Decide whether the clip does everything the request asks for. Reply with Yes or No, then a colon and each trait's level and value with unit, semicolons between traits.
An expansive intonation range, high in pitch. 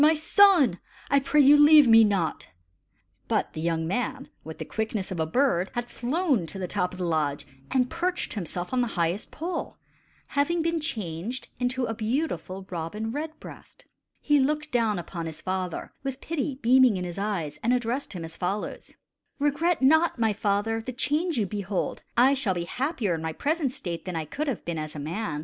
Yes: wide, 7.9 semitones; high, 225 Hz